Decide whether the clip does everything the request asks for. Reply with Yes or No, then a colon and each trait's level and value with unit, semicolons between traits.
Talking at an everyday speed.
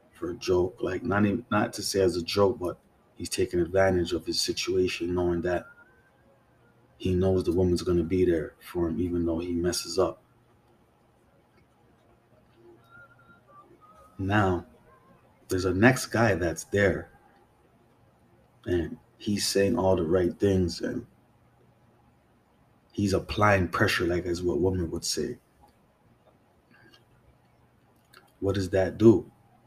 No: slow, 125 wpm